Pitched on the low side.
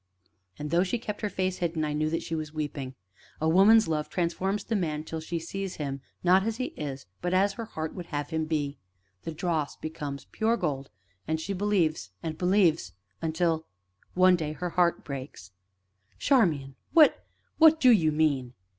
No: medium, 165 Hz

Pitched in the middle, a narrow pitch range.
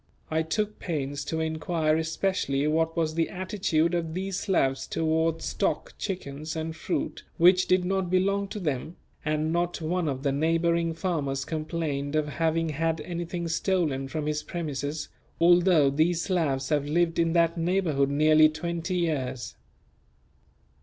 Yes: medium, 160 Hz; narrow, 2.3 semitones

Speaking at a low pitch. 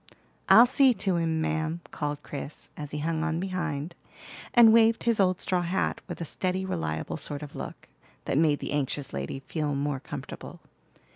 No: medium, 160 Hz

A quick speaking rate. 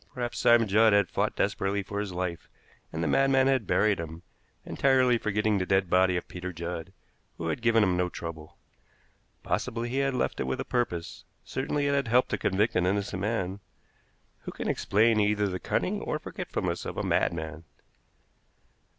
No: average, 180 wpm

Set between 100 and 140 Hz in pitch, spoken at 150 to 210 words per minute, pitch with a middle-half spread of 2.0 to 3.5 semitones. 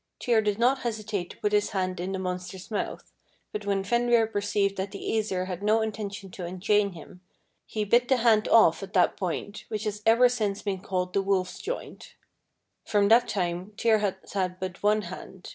No: high, 205 Hz; average, 195 wpm; average, 2.7 semitones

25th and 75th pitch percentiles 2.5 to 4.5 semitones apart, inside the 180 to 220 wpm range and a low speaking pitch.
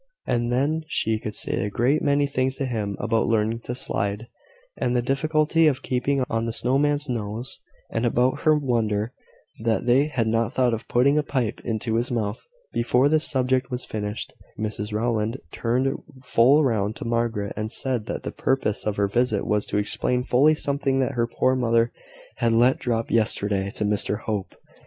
Yes: average, 3.4 semitones; average, 185 wpm; low, 120 Hz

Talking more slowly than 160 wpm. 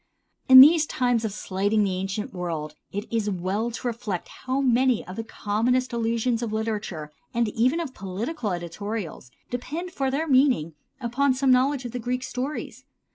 No: average, 175 wpm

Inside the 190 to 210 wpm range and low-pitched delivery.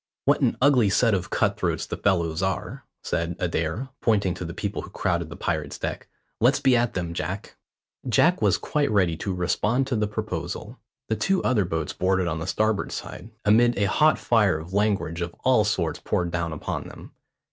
Yes: average, 195 wpm; very low, 95 Hz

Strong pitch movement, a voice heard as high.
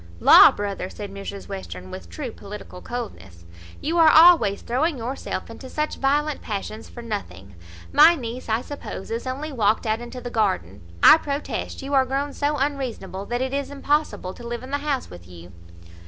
Yes: wide, 6.0 semitones; high, 240 Hz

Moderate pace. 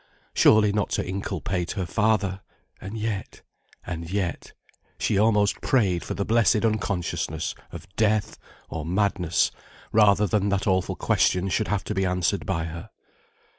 Yes: average, 145 wpm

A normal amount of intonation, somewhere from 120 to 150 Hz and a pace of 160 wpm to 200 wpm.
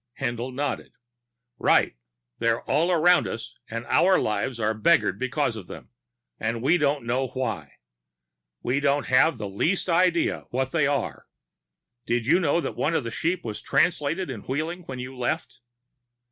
No: wide, 5.7 semitones; low, 135 Hz; average, 170 wpm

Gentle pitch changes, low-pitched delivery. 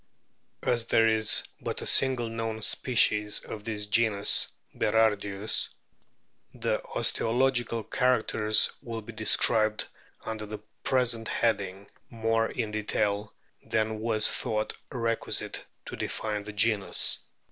Yes: narrow, 1.4 semitones; low, 110 Hz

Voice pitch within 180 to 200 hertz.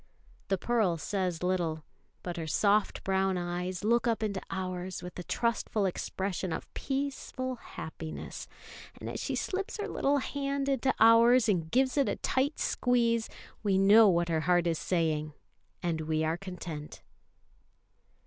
Yes: high, 190 Hz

